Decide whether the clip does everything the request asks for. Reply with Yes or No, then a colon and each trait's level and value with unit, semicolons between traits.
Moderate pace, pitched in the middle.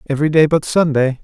Yes: average, 195 wpm; medium, 150 Hz